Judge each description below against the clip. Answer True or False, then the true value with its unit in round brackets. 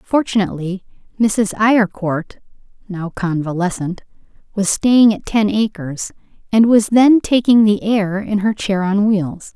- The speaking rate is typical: False (130 wpm)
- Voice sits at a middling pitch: False (205 Hz)